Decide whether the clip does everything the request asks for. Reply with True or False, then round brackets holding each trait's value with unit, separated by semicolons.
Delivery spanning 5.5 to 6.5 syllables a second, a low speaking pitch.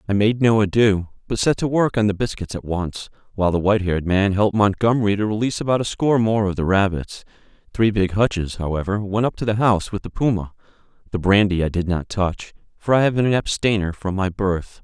True (6.0 syllables/s; 100 Hz)